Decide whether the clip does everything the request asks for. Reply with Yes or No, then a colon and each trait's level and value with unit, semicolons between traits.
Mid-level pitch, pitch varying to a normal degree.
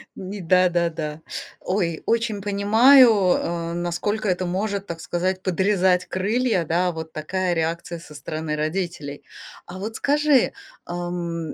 Yes: medium, 180 Hz; average, 3.2 semitones